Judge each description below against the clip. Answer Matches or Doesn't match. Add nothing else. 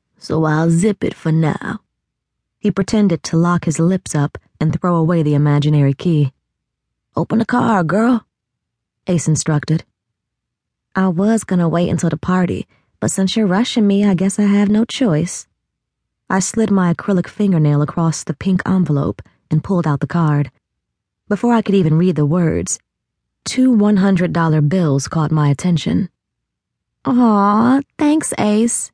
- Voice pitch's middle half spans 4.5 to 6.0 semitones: Matches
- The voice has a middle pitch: Matches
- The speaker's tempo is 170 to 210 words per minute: Doesn't match